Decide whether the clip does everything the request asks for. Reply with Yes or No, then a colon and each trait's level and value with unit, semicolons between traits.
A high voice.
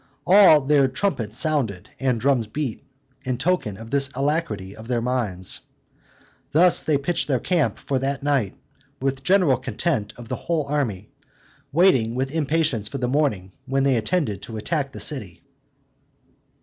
No: low, 135 Hz